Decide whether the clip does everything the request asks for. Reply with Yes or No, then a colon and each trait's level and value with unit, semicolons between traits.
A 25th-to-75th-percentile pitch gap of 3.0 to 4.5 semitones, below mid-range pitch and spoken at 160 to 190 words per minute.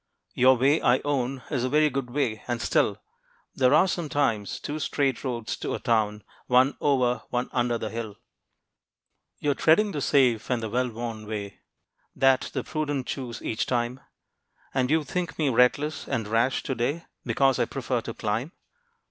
Yes: average, 3.4 semitones; low, 125 Hz; average, 175 wpm